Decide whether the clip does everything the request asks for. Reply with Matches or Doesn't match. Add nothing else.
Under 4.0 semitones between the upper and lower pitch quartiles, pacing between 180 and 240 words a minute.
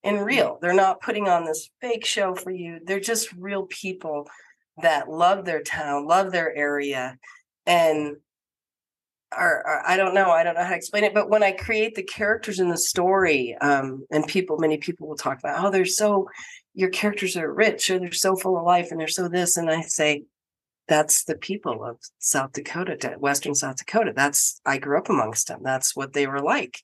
Doesn't match